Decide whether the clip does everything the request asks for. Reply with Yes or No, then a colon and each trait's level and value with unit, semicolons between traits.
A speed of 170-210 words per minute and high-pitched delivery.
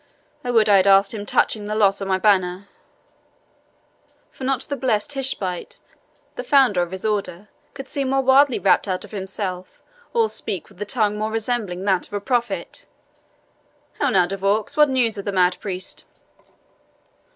Yes: average, 175 wpm; high, 205 Hz